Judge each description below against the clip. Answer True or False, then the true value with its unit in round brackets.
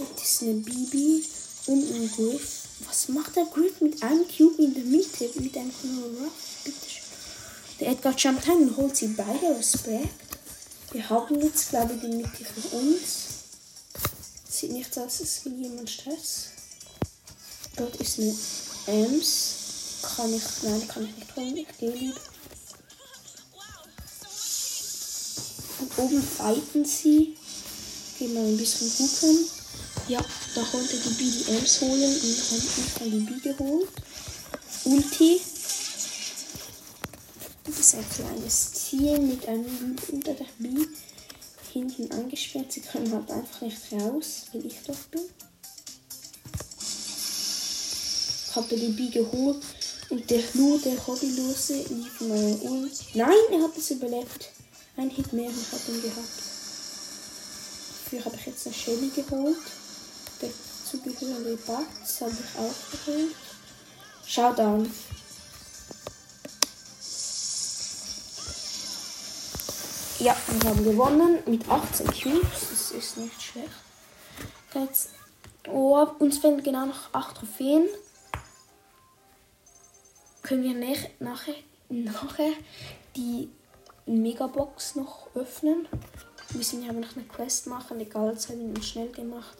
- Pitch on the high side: True (260 Hz)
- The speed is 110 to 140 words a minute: True (125 wpm)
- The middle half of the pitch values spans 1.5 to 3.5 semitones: False (3.9 semitones)